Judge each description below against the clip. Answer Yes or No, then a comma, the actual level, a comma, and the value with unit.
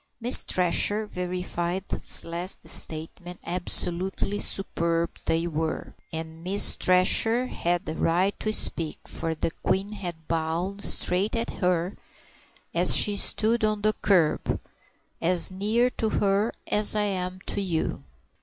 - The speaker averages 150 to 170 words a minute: No, slow, 135 wpm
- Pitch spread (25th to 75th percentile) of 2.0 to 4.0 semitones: Yes, average, 3.4 semitones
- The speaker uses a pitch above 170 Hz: Yes, medium, 185 Hz